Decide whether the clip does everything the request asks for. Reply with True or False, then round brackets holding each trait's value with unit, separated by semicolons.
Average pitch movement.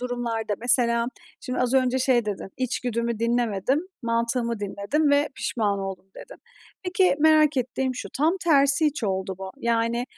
True (3.1 semitones)